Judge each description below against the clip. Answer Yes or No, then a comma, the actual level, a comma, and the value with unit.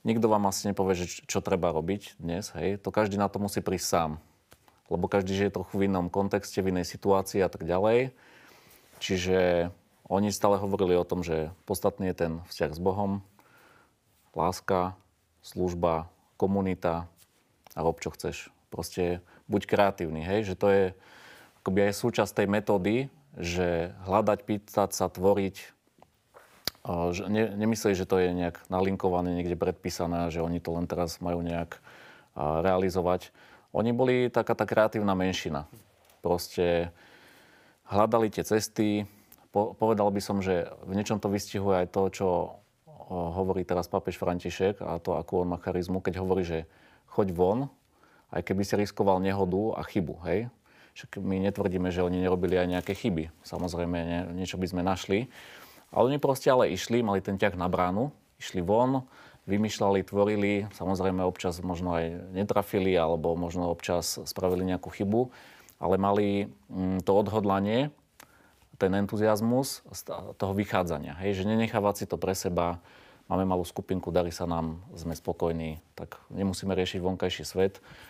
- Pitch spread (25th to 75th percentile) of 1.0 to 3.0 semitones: Yes, narrow, 2.4 semitones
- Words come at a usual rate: Yes, average, 150 wpm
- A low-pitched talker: Yes, very low, 95 Hz